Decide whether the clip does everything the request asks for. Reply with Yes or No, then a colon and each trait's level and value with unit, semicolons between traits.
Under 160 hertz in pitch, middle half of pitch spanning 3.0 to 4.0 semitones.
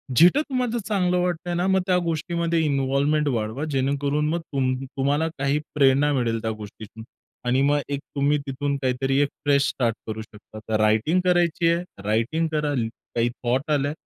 No: medium, 140 Hz; average, 4.4 semitones